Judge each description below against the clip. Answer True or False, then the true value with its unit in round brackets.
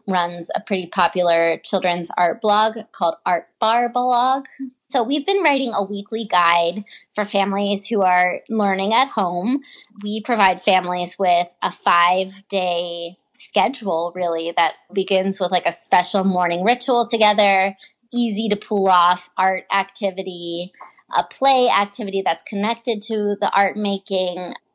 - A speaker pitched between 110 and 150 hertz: False (195 Hz)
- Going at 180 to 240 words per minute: False (140 wpm)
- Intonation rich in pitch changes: False (3.8 semitones)